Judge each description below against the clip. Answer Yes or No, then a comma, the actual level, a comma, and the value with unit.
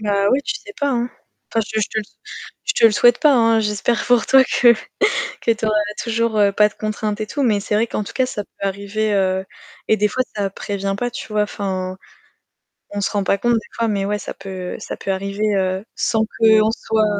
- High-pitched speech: Yes, high, 215 Hz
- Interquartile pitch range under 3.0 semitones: Yes, narrow, 2.4 semitones